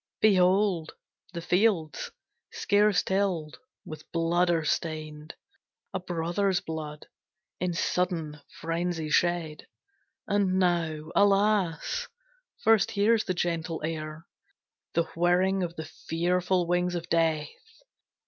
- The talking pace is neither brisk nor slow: No, slow, 105 wpm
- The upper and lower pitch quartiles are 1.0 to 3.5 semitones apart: Yes, average, 2.8 semitones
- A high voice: No, medium, 175 Hz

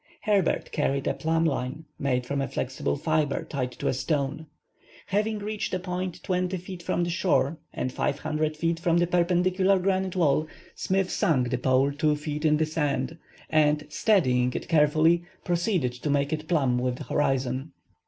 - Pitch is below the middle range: No, medium, 155 Hz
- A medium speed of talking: Yes, average, 175 wpm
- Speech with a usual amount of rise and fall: Yes, average, 4.3 semitones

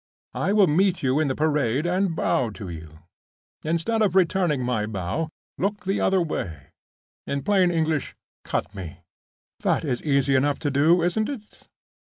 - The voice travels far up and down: Yes, wide, 6.2 semitones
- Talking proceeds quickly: No, average, 160 wpm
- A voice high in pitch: No, medium, 155 Hz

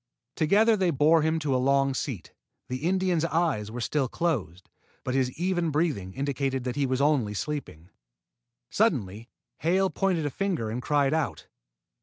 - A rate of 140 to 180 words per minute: Yes, average, 160 wpm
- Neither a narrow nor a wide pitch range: Yes, average, 4.7 semitones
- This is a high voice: No, medium, 145 Hz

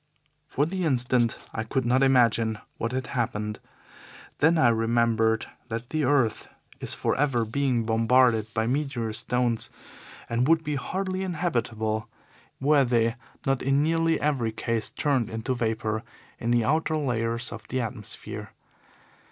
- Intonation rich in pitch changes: No, average, 3.8 semitones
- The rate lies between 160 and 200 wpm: No, average, 145 wpm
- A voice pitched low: Yes, low, 120 Hz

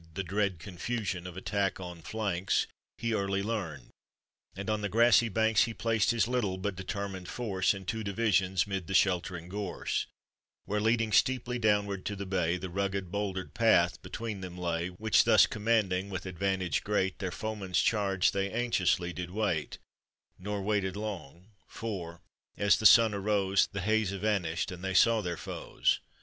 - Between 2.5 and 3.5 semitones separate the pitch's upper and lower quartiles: Yes, average, 2.8 semitones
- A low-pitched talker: Yes, low, 100 Hz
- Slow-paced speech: No, average, 165 wpm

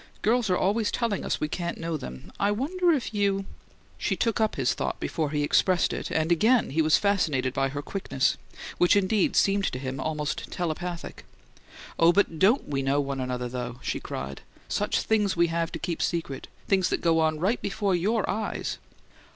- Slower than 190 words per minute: No, average, 195 wpm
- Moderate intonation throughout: No, wide, 5.8 semitones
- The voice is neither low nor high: Yes, medium, 170 Hz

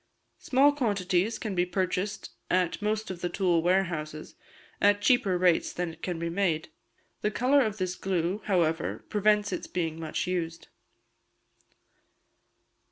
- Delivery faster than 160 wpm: No, average, 140 wpm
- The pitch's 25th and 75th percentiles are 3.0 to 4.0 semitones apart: Yes, average, 3.3 semitones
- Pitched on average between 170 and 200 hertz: Yes, medium, 185 Hz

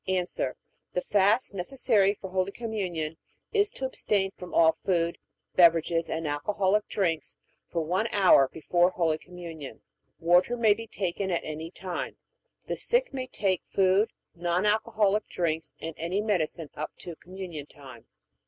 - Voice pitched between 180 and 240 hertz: Yes, medium, 185 Hz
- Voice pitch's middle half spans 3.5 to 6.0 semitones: Yes, average, 3.8 semitones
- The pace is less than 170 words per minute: Yes, average, 145 wpm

